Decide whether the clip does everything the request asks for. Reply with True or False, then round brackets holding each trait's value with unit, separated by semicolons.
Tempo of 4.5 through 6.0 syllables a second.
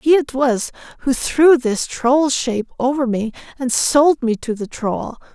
False (4.0 syllables/s)